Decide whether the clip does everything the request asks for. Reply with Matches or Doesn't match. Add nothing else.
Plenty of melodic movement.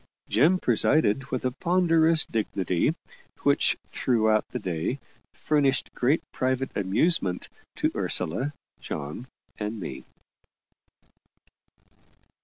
Matches